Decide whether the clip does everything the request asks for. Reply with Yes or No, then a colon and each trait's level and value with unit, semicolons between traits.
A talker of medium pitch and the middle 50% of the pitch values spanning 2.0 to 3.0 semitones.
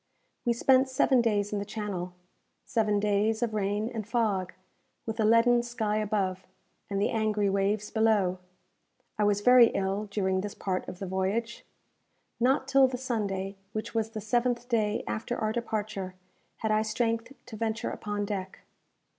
No: high, 215 Hz; narrow, 2.5 semitones